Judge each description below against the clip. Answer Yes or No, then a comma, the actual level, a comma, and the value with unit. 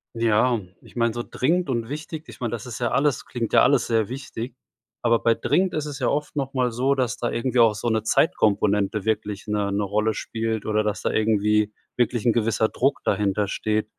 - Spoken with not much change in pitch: No, average, 3.1 semitones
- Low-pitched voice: Yes, low, 115 Hz